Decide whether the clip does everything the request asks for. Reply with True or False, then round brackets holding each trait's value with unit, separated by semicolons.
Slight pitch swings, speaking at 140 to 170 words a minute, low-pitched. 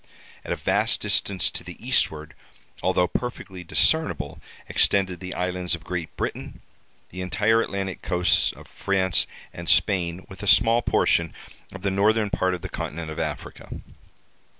True (2.2 semitones; 150 wpm; 95 Hz)